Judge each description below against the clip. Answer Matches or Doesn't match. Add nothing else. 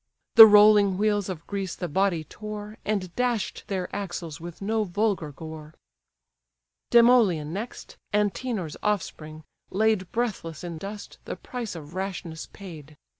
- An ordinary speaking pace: Doesn't match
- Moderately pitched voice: Doesn't match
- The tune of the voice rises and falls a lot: Doesn't match